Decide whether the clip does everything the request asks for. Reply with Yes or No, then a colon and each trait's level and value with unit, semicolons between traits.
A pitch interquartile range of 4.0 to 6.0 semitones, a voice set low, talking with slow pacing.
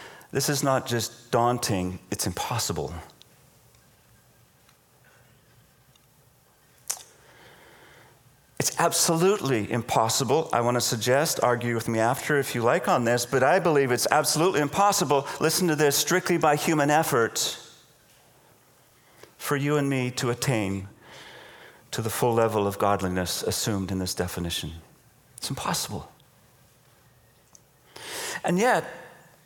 Yes: average, 4.5 semitones; low, 130 Hz; slow, 115 wpm